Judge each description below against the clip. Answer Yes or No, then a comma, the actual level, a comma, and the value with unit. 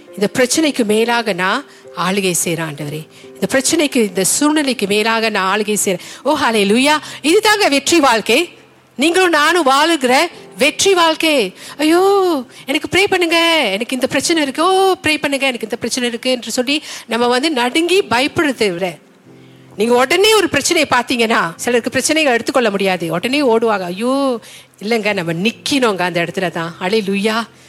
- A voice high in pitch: Yes, high, 245 Hz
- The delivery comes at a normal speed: No, fast, 140 wpm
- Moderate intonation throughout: No, wide, 6.9 semitones